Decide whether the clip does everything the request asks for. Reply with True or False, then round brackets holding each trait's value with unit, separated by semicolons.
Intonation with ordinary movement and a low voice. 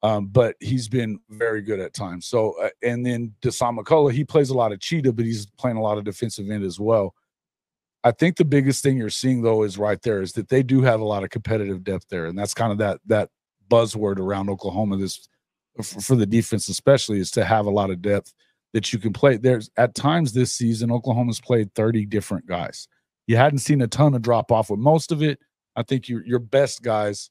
True (3.6 semitones; 115 Hz)